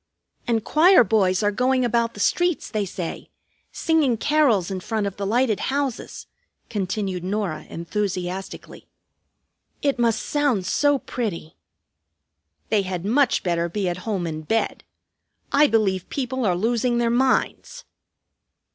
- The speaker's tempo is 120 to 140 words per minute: Yes, slow, 135 wpm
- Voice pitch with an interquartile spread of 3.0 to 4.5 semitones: No, average, 5.3 semitones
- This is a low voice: No, high, 220 Hz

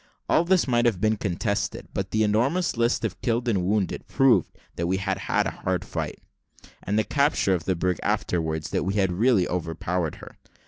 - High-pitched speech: No, low, 100 Hz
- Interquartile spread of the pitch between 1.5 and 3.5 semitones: No, average, 4.7 semitones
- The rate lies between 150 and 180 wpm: No, average, 195 wpm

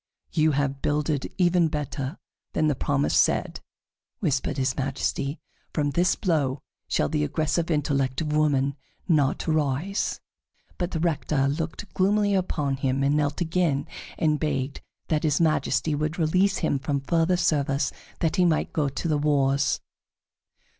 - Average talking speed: Yes, average, 145 wpm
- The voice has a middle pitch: Yes, medium, 150 Hz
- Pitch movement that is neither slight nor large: Yes, average, 3.0 semitones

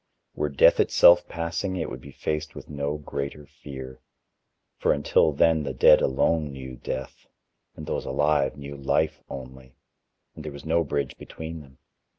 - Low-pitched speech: Yes, very low, 70 Hz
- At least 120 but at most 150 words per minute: No, average, 160 wpm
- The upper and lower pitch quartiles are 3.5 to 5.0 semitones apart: No, narrow, 2.6 semitones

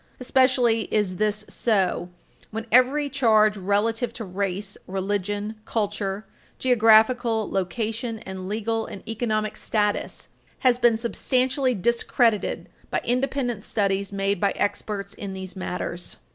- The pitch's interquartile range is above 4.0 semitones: No, average, 3.0 semitones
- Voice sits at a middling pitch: No, high, 215 Hz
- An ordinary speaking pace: No, slow, 115 wpm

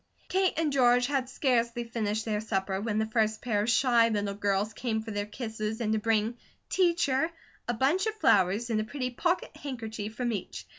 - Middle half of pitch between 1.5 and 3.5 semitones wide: Yes, average, 3.1 semitones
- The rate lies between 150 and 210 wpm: Yes, average, 195 wpm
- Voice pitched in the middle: No, high, 225 Hz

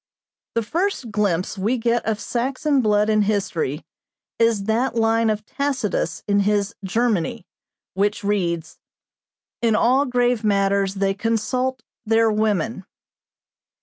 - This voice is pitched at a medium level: No, high, 215 Hz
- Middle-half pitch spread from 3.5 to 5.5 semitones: No, average, 2.9 semitones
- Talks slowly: Yes, slow, 120 wpm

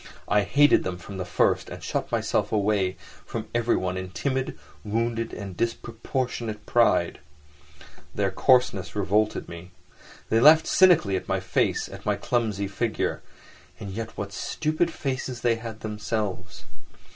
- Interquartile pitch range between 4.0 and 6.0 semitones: No, average, 3.4 semitones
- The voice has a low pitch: Yes, low, 110 Hz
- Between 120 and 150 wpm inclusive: Yes, average, 140 wpm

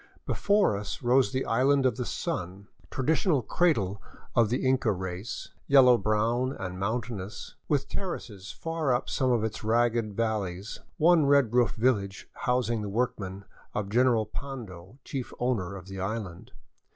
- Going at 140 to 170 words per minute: Yes, average, 150 wpm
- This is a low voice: Yes, low, 115 Hz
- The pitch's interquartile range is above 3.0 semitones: Yes, average, 4.5 semitones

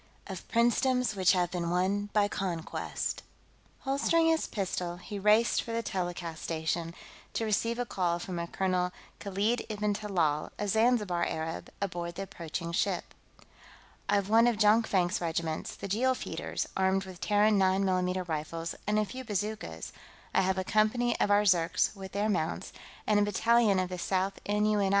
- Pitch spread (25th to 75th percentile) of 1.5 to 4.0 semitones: Yes, average, 3.2 semitones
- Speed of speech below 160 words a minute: No, average, 165 wpm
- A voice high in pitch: Yes, high, 195 Hz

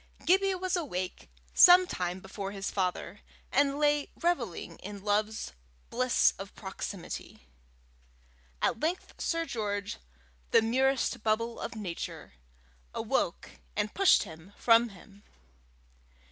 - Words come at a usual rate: No, slow, 115 wpm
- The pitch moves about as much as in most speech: No, wide, 6.6 semitones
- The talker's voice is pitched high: Yes, high, 220 Hz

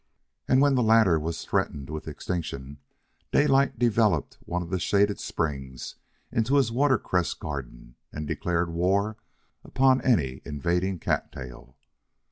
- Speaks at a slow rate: Yes, slow, 130 wpm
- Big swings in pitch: Yes, wide, 7.4 semitones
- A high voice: No, very low, 90 Hz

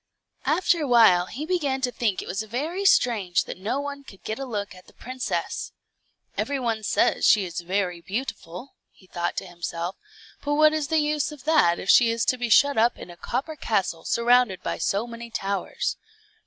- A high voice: Yes, high, 235 Hz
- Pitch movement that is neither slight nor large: No, wide, 6.6 semitones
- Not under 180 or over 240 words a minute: Yes, average, 200 wpm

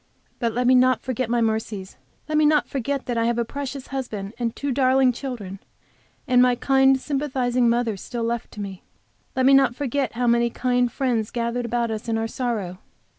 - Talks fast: No, average, 195 wpm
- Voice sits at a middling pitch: No, high, 245 Hz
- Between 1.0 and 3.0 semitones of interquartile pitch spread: Yes, narrow, 2.4 semitones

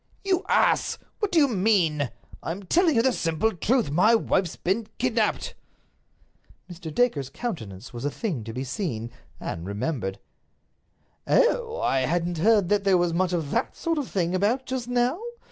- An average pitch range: No, wide, 8.0 semitones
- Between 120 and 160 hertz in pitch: No, medium, 185 Hz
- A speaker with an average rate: Yes, average, 165 wpm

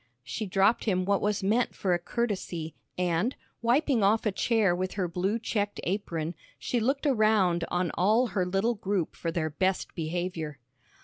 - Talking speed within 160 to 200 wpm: Yes, average, 170 wpm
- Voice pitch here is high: Yes, high, 195 Hz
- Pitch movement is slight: No, average, 3.9 semitones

